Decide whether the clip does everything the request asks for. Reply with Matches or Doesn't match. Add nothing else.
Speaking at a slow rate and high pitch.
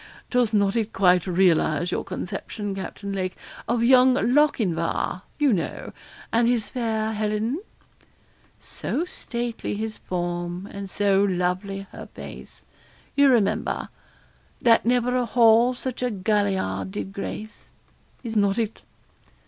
Matches